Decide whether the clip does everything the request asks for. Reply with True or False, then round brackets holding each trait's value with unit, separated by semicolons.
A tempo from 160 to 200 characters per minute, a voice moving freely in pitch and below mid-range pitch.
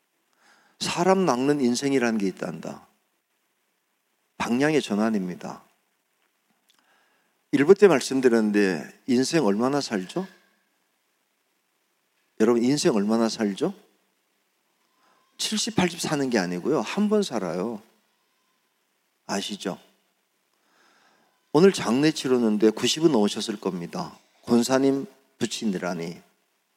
True (190 characters per minute; 8.7 semitones; 130 Hz)